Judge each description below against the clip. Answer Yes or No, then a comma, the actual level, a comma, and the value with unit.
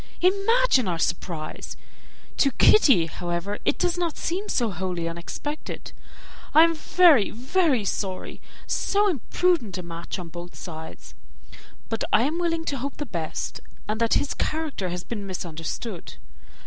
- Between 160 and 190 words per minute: No, average, 145 wpm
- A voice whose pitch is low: No, high, 230 Hz